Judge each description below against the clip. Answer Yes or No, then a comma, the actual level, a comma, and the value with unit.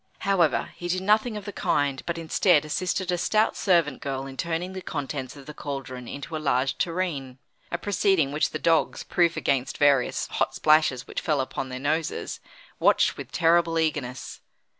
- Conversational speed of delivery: Yes, average, 180 wpm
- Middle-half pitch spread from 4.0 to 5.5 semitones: Yes, average, 4.3 semitones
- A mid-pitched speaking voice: Yes, medium, 155 Hz